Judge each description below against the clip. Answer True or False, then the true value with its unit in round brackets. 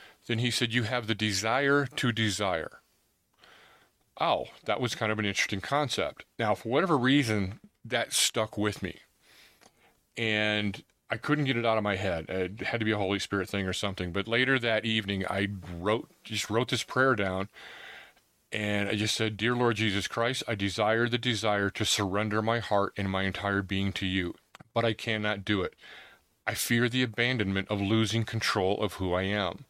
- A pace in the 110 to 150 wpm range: False (190 wpm)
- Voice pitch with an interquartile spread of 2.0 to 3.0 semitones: True (2.7 semitones)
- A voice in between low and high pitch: False (105 Hz)